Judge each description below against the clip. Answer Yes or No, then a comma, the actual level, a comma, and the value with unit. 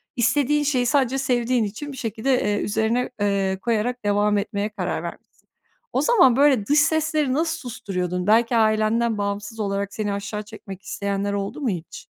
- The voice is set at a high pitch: Yes, high, 220 Hz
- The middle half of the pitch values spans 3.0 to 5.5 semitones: Yes, average, 4.1 semitones